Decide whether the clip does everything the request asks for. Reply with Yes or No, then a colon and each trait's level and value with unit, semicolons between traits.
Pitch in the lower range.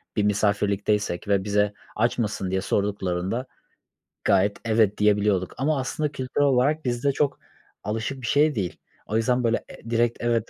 Yes: low, 110 Hz